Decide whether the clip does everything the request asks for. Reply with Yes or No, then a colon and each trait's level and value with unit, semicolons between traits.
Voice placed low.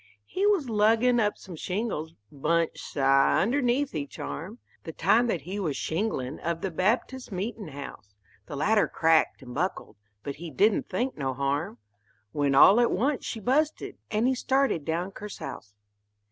No: medium, 185 Hz